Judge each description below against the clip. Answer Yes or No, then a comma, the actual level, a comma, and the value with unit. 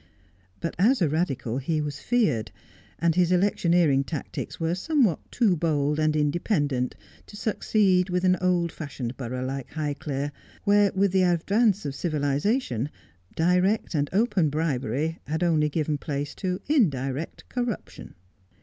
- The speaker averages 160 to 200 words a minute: No, average, 140 wpm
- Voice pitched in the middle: Yes, medium, 165 Hz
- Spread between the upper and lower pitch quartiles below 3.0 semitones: No, average, 4.5 semitones